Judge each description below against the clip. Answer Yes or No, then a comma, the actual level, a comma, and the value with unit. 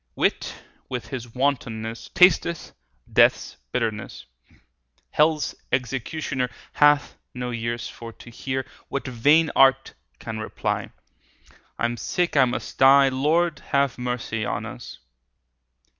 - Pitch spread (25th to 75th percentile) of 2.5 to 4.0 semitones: Yes, average, 3.5 semitones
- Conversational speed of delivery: No, slow, 120 wpm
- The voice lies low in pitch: Yes, low, 130 Hz